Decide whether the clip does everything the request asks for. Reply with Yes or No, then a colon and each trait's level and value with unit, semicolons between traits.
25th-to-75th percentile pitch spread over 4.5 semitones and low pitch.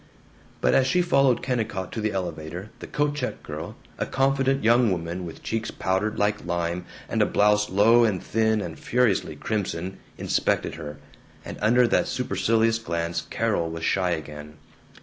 Yes: wide, 5.4 semitones; low, 105 Hz